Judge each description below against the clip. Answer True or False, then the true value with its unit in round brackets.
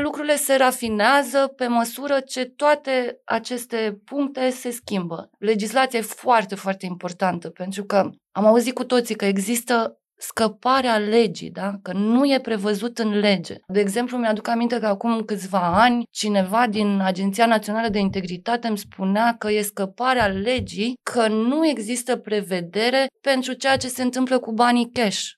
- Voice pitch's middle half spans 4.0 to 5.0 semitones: False (3.5 semitones)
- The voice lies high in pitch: True (230 Hz)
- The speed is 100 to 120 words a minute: False (155 wpm)